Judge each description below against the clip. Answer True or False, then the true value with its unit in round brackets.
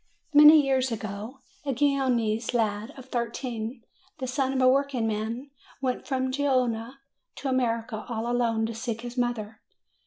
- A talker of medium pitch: False (245 Hz)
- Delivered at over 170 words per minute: False (145 wpm)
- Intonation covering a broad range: False (2.8 semitones)